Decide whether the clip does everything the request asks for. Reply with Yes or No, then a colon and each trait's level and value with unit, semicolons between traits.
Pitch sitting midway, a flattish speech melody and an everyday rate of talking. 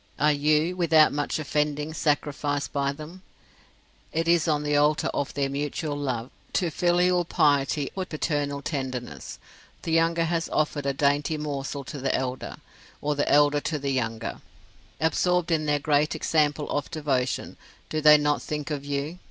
Yes: medium, 150 Hz; narrow, 1.9 semitones; average, 160 wpm